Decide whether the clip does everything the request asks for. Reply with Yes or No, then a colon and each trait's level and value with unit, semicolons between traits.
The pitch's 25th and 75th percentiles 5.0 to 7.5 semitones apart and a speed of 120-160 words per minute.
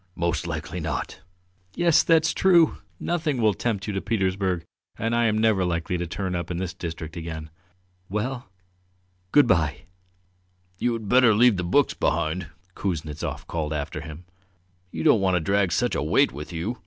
No: wide, 5.6 semitones; average, 170 wpm